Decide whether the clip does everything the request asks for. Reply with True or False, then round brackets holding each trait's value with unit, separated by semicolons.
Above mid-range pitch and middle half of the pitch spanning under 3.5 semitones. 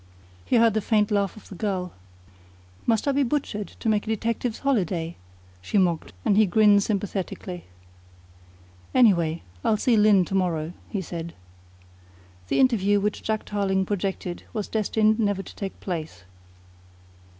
True (205 Hz; 3.0 semitones)